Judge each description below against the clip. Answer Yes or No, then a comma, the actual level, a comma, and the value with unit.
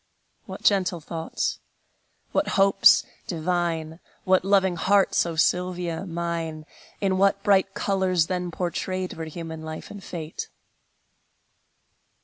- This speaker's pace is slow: Yes, slow, 115 wpm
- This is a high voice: No, medium, 180 Hz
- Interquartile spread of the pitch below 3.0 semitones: Yes, narrow, 2.6 semitones